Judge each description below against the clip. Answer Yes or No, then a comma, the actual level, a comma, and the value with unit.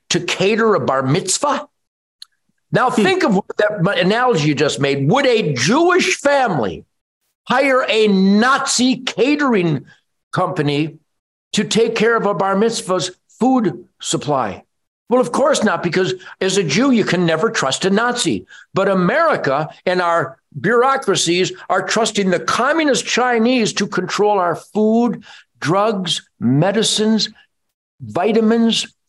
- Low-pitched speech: No, high, 205 Hz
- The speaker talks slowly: Yes, slow, 130 wpm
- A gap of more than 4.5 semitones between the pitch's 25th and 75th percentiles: Yes, average, 4.9 semitones